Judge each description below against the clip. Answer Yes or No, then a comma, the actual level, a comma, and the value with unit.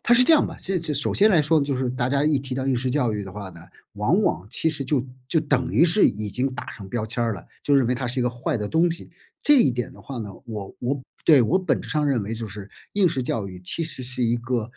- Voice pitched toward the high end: No, low, 130 Hz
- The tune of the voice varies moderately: Yes, average, 4.7 semitones